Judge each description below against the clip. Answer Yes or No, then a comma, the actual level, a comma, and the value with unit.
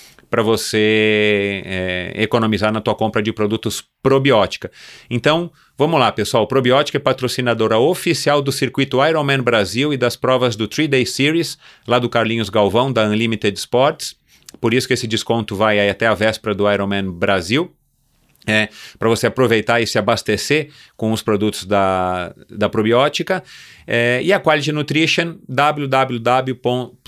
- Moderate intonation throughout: Yes, average, 3.9 semitones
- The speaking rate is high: No, average, 150 wpm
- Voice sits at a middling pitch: No, low, 115 Hz